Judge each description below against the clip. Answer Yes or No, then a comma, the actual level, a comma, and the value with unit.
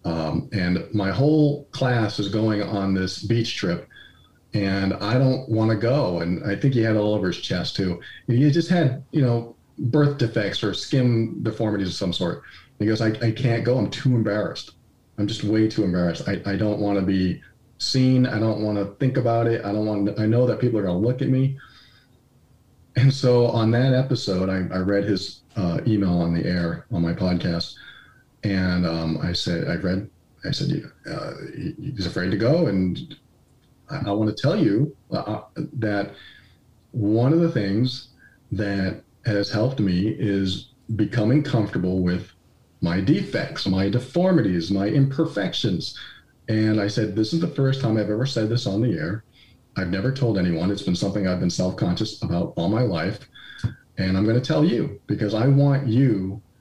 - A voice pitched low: Yes, low, 110 Hz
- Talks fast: No, average, 195 wpm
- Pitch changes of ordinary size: Yes, average, 4.3 semitones